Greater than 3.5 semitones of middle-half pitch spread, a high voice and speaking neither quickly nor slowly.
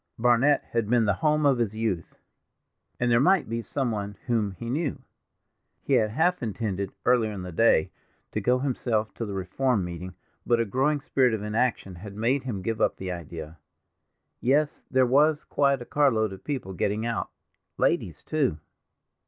No: average, 4.7 semitones; low, 115 Hz; average, 175 wpm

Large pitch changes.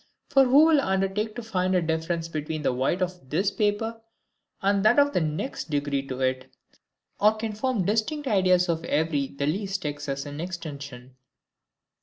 Yes: wide, 6.4 semitones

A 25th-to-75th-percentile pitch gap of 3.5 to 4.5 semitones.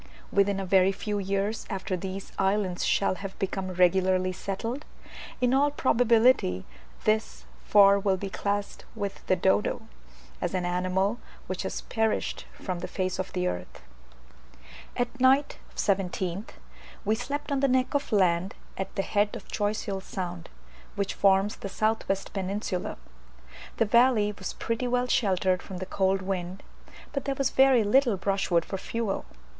No: average, 3.0 semitones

